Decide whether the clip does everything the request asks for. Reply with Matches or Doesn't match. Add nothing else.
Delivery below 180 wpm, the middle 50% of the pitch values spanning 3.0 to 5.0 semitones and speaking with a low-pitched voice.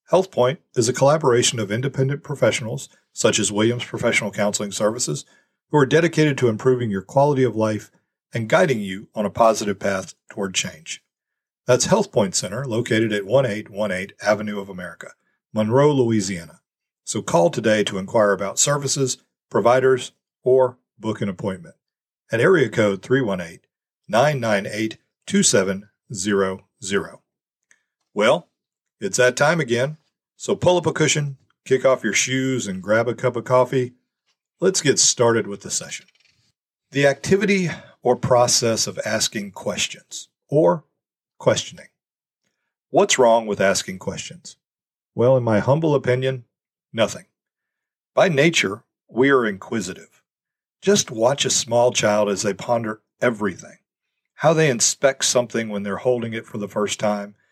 Matches